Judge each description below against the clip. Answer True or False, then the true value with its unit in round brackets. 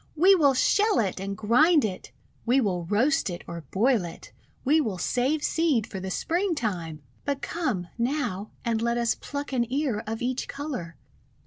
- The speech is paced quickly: False (175 wpm)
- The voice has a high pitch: True (240 Hz)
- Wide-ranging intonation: True (6.7 semitones)